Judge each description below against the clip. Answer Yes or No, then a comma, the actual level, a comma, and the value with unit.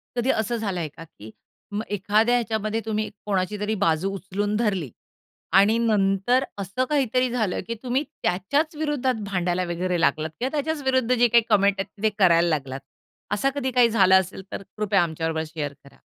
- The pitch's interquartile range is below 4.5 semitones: No, average, 4.8 semitones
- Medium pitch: No, high, 205 Hz